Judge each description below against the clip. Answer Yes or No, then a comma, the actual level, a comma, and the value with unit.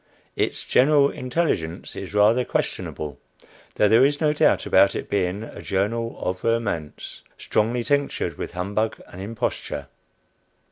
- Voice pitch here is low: Yes, low, 110 Hz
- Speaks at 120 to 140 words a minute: Yes, slow, 135 wpm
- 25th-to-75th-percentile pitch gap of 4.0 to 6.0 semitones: Yes, average, 4.8 semitones